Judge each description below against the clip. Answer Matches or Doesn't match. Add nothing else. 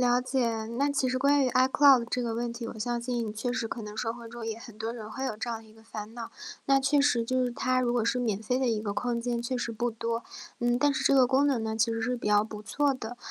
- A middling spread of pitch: Doesn't match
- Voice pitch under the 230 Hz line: Doesn't match